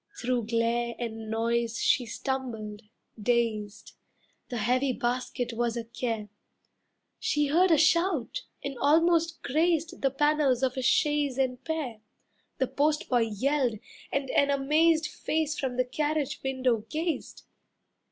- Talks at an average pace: No, slow, 130 wpm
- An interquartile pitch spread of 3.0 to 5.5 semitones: Yes, average, 4.2 semitones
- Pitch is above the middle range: Yes, very high, 260 Hz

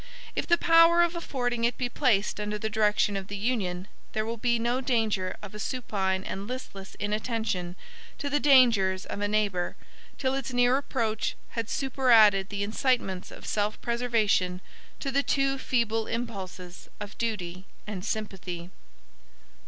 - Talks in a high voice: Yes, high, 220 Hz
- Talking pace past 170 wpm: No, average, 155 wpm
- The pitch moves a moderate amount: Yes, average, 4.1 semitones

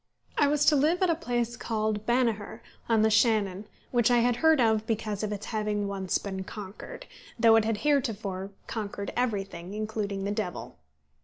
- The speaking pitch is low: No, high, 220 Hz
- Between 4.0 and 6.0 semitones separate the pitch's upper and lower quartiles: No, average, 3.0 semitones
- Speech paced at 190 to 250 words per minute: No, average, 175 wpm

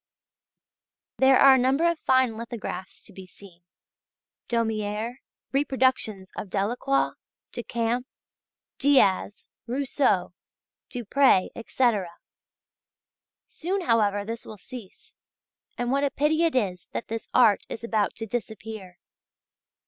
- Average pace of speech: No, slow, 110 wpm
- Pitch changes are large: No, average, 4.3 semitones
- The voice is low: No, high, 235 Hz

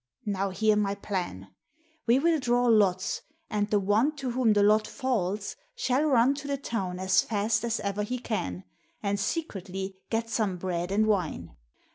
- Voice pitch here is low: No, high, 210 Hz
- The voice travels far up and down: No, average, 3.8 semitones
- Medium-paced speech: Yes, average, 170 wpm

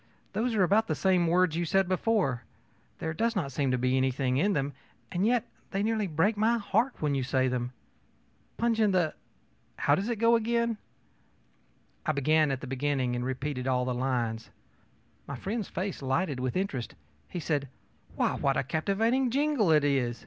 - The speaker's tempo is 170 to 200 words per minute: Yes, average, 185 wpm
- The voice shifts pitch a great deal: Yes, wide, 8.1 semitones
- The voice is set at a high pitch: No, medium, 160 Hz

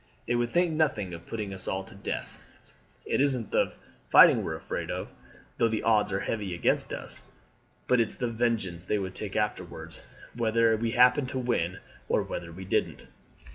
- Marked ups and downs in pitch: No, average, 3.9 semitones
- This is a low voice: Yes, low, 110 Hz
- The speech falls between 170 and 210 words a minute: Yes, average, 185 wpm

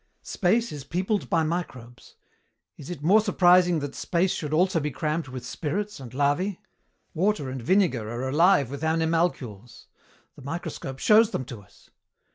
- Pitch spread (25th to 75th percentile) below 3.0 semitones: No, average, 5.3 semitones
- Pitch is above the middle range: No, medium, 160 Hz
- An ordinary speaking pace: Yes, average, 155 wpm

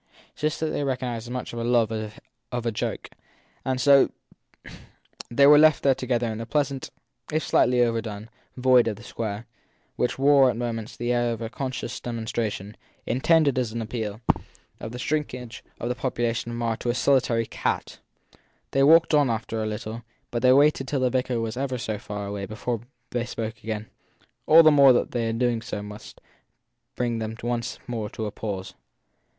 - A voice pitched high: No, low, 120 Hz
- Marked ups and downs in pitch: No, narrow, 2.6 semitones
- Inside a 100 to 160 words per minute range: No, average, 190 wpm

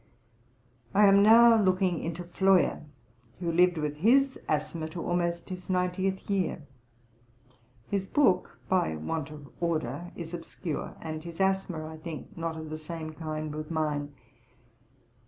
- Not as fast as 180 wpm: Yes, average, 140 wpm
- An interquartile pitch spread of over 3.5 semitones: No, average, 3.1 semitones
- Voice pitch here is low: No, medium, 170 Hz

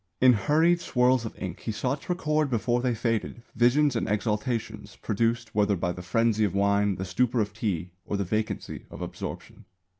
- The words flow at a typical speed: Yes, average, 185 wpm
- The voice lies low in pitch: Yes, low, 115 Hz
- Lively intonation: No, average, 3.5 semitones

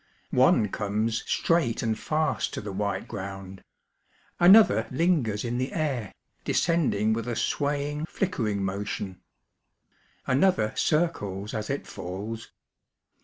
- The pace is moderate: No, slow, 115 wpm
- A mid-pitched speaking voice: No, low, 115 Hz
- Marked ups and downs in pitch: Yes, wide, 6.3 semitones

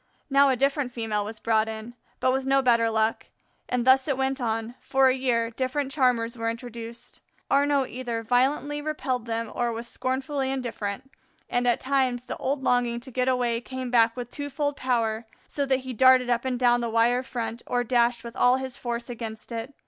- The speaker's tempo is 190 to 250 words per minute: Yes, average, 195 wpm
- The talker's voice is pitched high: Yes, high, 245 Hz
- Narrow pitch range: Yes, narrow, 2.2 semitones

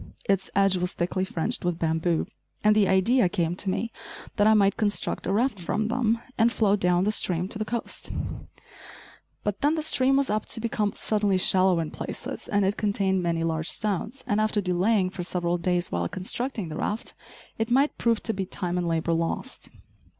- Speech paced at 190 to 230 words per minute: Yes, average, 195 wpm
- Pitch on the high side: Yes, high, 195 Hz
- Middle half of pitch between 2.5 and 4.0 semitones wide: Yes, average, 3.6 semitones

